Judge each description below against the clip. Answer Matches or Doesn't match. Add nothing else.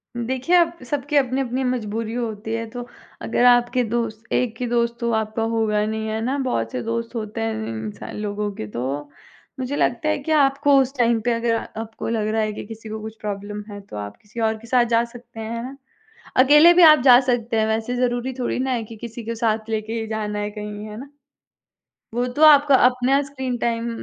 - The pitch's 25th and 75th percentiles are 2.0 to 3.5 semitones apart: Matches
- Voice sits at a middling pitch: Doesn't match